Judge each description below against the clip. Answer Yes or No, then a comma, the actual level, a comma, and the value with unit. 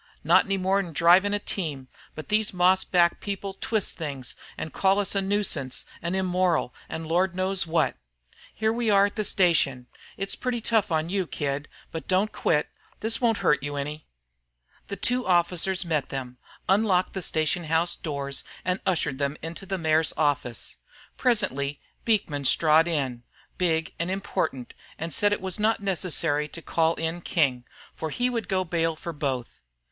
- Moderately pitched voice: Yes, medium, 170 Hz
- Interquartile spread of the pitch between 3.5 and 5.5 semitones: Yes, average, 4.3 semitones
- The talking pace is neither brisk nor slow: Yes, average, 170 wpm